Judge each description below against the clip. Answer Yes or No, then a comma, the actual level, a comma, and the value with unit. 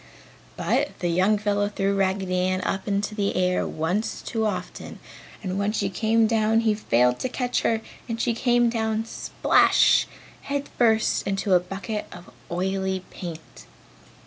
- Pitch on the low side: No, high, 200 Hz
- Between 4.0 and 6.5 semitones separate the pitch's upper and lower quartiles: No, average, 3.2 semitones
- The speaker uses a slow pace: No, average, 155 wpm